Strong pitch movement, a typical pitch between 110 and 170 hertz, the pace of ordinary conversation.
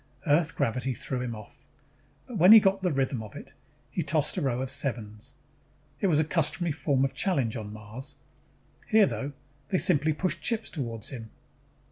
Yes: wide, 5.9 semitones; medium, 140 Hz; average, 180 wpm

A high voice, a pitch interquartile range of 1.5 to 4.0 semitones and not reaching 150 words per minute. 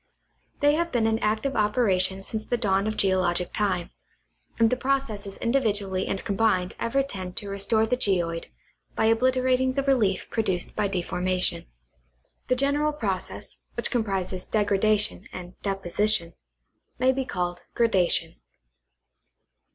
No: high, 210 Hz; average, 4.6 semitones; slow, 135 wpm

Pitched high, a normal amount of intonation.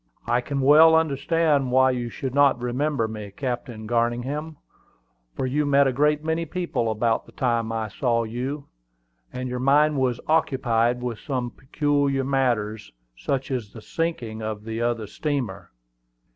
No: low, 130 Hz; average, 3.5 semitones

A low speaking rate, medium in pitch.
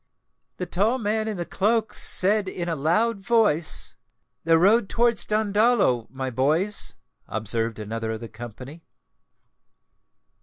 Yes: slow, 125 wpm; medium, 175 Hz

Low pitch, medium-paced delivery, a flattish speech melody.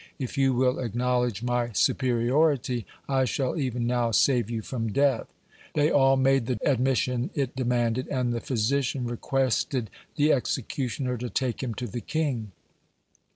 Yes: low, 125 Hz; average, 150 wpm; narrow, 2.1 semitones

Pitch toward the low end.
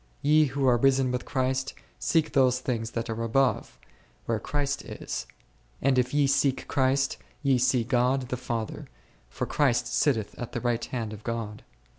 Yes: low, 130 Hz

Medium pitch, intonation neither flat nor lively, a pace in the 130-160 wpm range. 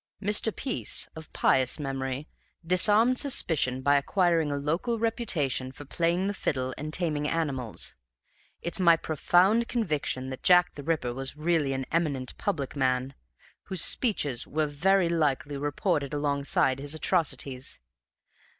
Yes: medium, 150 Hz; average, 4.6 semitones; average, 140 wpm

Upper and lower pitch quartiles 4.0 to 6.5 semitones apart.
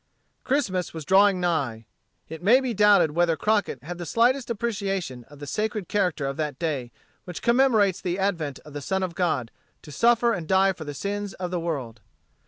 Yes: average, 5.2 semitones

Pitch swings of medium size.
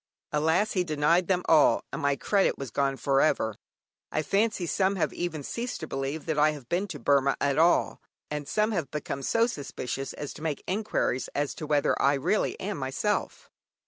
Yes: average, 4.7 semitones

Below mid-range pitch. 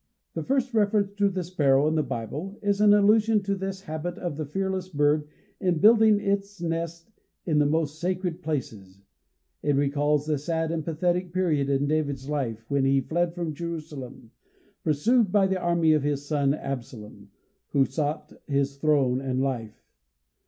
No: medium, 155 Hz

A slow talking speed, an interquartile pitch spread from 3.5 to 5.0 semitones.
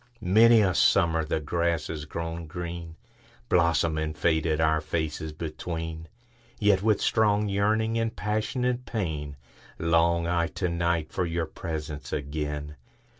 Yes: slow, 120 wpm; average, 4.5 semitones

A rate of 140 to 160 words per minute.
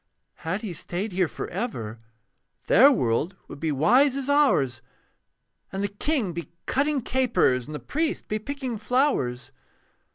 Yes: average, 150 wpm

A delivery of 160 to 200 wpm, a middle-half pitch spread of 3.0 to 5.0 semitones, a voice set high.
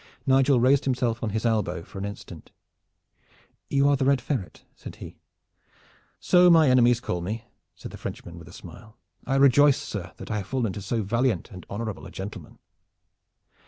No: average, 180 wpm; average, 4.7 semitones; low, 120 Hz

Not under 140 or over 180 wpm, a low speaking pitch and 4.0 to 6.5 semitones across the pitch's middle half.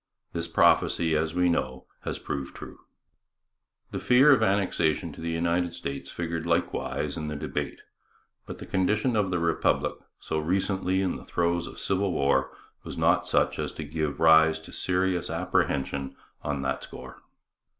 No: average, 160 wpm; very low, 85 Hz; average, 3.3 semitones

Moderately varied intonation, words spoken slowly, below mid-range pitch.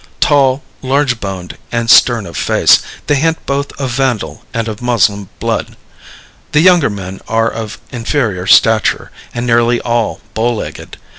No: average, 3.5 semitones; average, 150 wpm; low, 120 Hz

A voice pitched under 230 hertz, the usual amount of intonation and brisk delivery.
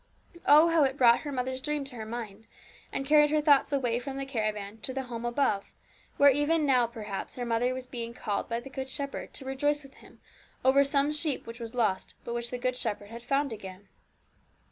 No: very high, 255 Hz; average, 3.3 semitones; fast, 215 wpm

